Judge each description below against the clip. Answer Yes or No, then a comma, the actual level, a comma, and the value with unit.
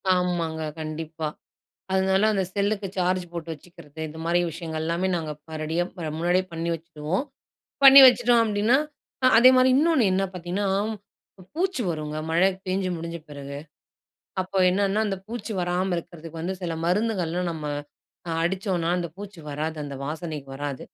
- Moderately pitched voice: Yes, medium, 175 Hz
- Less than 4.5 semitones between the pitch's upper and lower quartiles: Yes, average, 3.4 semitones